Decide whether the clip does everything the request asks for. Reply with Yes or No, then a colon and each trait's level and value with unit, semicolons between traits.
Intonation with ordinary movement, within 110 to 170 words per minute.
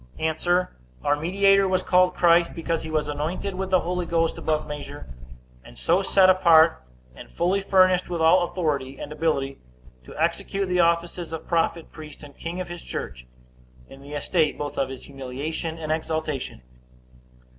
Yes: average, 3.2 semitones; average, 165 wpm